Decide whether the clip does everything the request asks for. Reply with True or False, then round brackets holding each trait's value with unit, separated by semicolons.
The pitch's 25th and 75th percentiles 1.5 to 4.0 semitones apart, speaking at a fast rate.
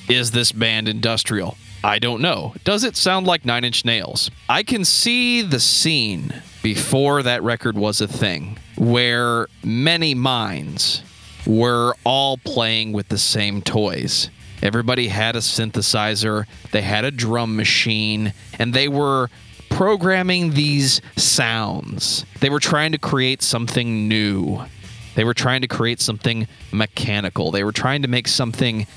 False (3.6 semitones; 145 wpm)